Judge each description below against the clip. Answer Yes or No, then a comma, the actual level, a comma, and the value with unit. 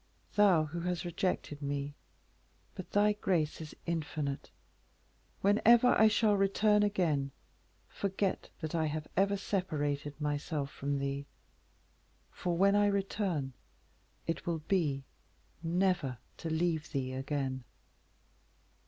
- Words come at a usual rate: No, slow, 115 wpm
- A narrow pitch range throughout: No, average, 5.2 semitones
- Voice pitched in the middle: Yes, medium, 165 Hz